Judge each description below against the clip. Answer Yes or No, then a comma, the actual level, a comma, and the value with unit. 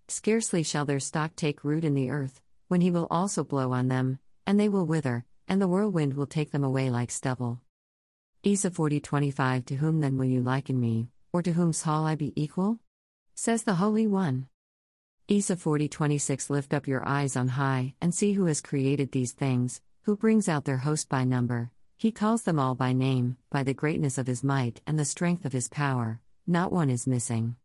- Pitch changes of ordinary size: Yes, average, 4.6 semitones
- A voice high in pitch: No, medium, 140 Hz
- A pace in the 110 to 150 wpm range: No, average, 200 wpm